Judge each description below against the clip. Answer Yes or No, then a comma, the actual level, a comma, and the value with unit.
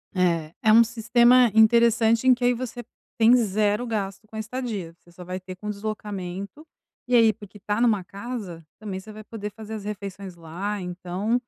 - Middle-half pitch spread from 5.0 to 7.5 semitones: No, average, 3.4 semitones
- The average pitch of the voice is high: Yes, high, 210 Hz